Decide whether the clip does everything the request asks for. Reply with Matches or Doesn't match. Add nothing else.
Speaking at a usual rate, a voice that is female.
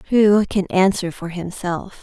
Matches